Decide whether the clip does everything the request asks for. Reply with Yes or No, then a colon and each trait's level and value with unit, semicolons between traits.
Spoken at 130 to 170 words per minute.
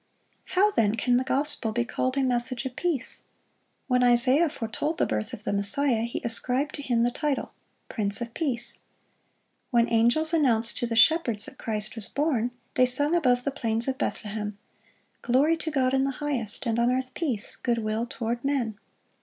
No: average, 185 wpm